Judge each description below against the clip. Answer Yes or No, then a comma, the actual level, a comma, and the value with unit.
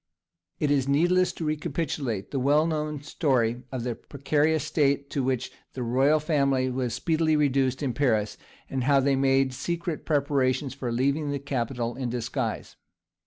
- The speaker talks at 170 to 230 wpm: No, average, 160 wpm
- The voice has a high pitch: No, medium, 140 Hz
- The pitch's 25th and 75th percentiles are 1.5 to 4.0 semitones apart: Yes, average, 2.8 semitones